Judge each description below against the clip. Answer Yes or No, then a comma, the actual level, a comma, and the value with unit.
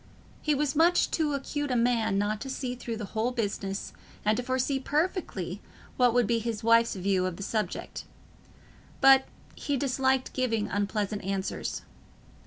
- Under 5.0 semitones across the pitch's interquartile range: Yes, average, 4.3 semitones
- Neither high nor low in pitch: No, high, 235 Hz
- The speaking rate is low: No, average, 160 wpm